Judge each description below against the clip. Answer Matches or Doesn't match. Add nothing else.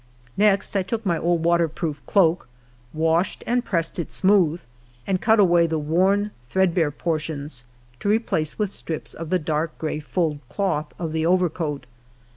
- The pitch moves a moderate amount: Matches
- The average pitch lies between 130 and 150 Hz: Doesn't match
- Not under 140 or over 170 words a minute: Matches